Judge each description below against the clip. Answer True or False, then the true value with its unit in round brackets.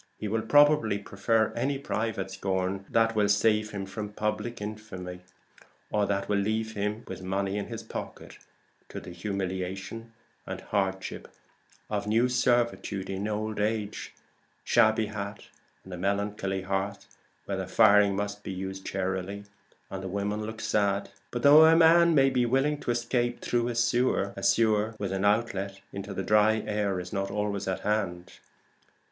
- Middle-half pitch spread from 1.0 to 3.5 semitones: True (2.5 semitones)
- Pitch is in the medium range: False (105 Hz)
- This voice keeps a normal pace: True (165 wpm)